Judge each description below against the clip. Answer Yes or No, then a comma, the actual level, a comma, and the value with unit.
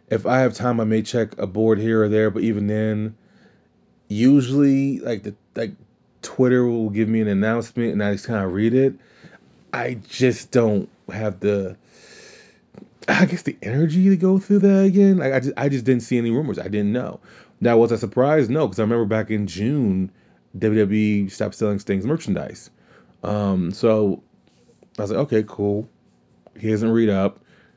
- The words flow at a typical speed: Yes, average, 185 wpm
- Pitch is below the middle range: Yes, low, 110 Hz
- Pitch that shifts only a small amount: No, average, 3.5 semitones